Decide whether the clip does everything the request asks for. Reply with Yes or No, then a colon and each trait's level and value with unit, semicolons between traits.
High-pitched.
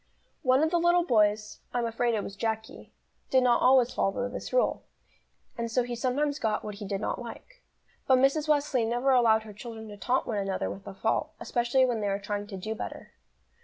Yes: high, 235 Hz